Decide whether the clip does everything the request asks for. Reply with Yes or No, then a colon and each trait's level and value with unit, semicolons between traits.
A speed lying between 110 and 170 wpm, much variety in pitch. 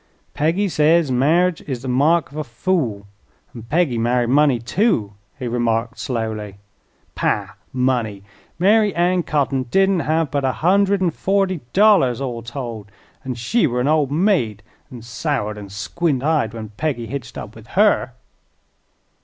Yes: average, 155 wpm; wide, 6.3 semitones